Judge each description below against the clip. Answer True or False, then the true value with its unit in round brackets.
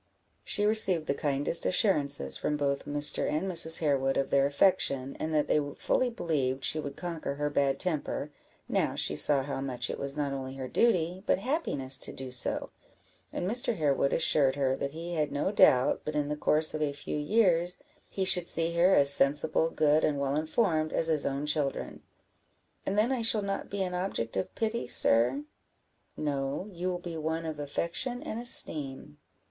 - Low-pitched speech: False (150 Hz)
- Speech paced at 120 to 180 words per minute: False (190 wpm)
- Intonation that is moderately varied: True (4.3 semitones)